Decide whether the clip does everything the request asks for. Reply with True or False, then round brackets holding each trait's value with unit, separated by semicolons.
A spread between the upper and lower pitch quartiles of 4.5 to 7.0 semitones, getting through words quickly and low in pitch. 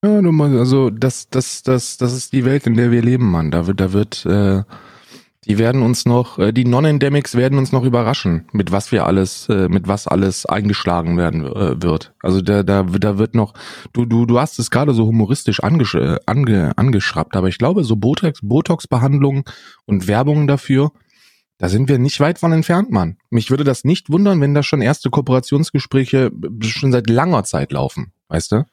True (5.2 semitones; 200 wpm; 120 Hz)